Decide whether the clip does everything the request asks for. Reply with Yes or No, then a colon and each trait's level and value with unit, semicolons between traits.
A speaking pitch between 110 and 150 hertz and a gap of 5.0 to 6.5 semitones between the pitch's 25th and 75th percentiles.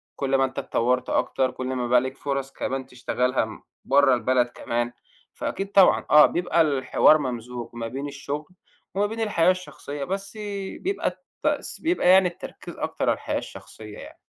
Yes: low, 135 Hz; wide, 5.6 semitones